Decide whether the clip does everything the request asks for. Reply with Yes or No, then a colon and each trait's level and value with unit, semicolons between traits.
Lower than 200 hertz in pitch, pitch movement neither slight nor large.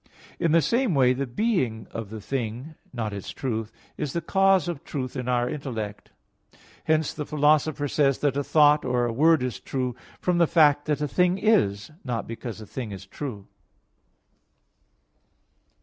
Yes: low, 135 Hz; average, 4.8 semitones